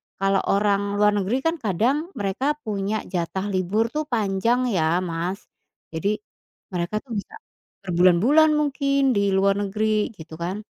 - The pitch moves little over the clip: No, average, 4.0 semitones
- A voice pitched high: Yes, high, 205 Hz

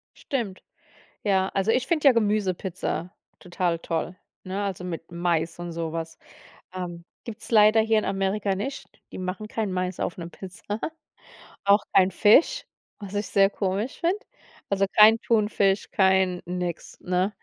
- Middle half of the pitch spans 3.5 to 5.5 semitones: No, average, 2.9 semitones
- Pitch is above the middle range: Yes, high, 195 Hz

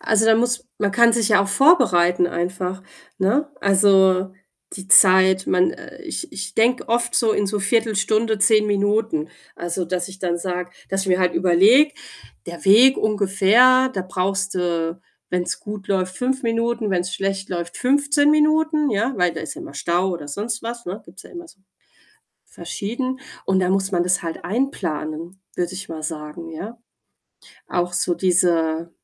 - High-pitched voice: Yes, high, 195 Hz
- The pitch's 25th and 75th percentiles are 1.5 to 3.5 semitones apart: No, average, 4.3 semitones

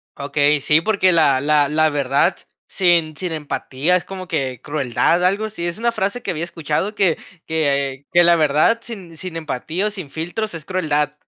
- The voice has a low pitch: No, medium, 165 Hz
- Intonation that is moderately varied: Yes, average, 4.0 semitones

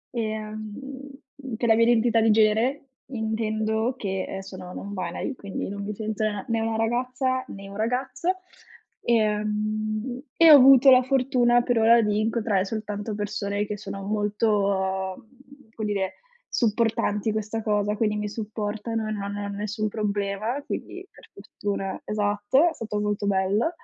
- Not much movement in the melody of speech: Yes, narrow, 2.2 semitones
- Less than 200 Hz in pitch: No, high, 215 Hz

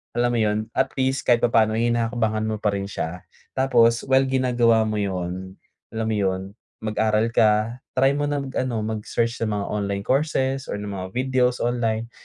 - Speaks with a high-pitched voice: No, low, 115 Hz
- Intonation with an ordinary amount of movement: Yes, average, 3.1 semitones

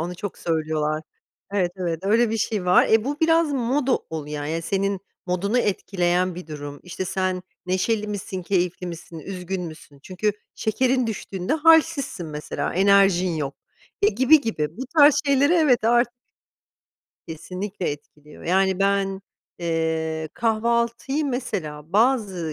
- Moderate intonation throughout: No, wide, 5.8 semitones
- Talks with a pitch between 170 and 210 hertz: Yes, high, 190 Hz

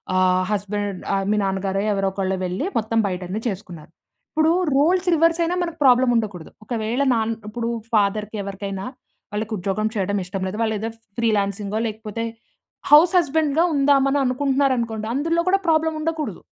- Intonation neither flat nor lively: No, wide, 6.1 semitones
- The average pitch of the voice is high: Yes, high, 220 Hz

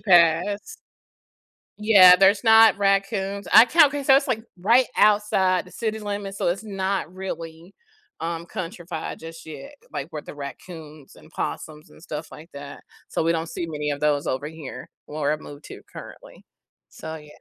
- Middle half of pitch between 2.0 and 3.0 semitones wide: No, average, 4.5 semitones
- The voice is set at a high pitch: No, medium, 180 Hz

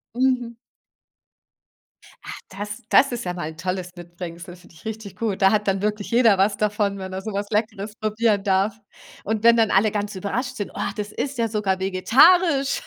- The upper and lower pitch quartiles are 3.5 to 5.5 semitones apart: No, average, 2.8 semitones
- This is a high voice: Yes, high, 205 Hz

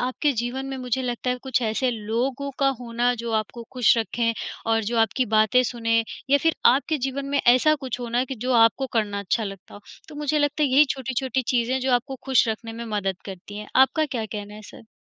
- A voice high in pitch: Yes, high, 245 Hz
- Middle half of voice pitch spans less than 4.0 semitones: Yes, average, 2.8 semitones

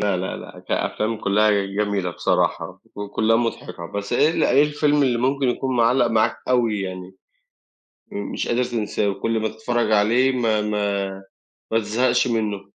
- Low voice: Yes, low, 110 Hz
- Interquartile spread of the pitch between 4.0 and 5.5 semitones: No, average, 3.1 semitones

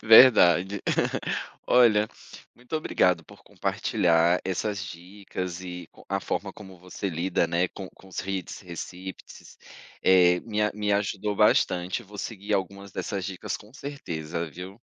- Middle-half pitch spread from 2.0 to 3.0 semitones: Yes, average, 2.7 semitones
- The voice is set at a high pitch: No, very low, 95 Hz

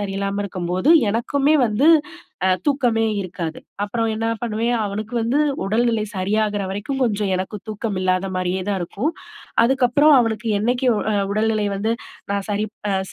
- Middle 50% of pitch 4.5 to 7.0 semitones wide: No, average, 3.0 semitones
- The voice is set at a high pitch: Yes, high, 215 Hz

